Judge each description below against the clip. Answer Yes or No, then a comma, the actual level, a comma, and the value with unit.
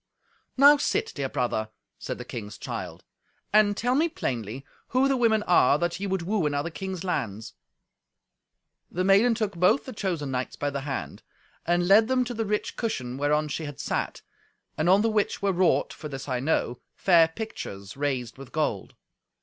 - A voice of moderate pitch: Yes, medium, 170 Hz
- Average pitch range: No, wide, 7.7 semitones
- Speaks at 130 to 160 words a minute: No, average, 185 wpm